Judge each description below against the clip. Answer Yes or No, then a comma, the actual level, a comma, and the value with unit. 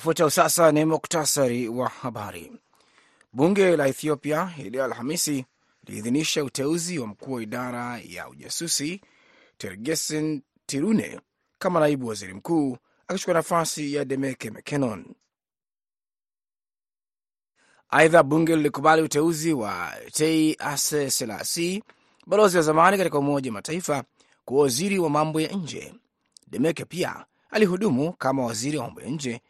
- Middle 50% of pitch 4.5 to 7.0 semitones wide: No, average, 4.0 semitones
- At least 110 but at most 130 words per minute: Yes, average, 120 wpm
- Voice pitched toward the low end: No, medium, 155 Hz